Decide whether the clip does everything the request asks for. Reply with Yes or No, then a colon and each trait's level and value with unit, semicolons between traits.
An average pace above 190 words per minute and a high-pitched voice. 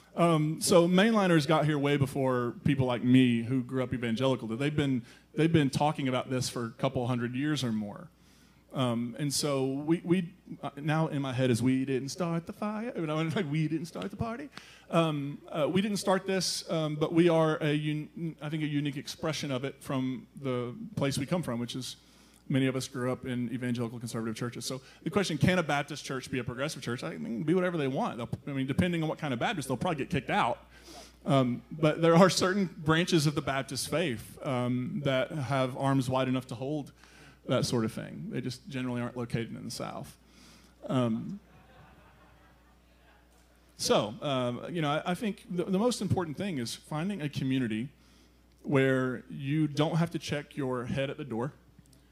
No: average, 200 wpm; medium, 140 Hz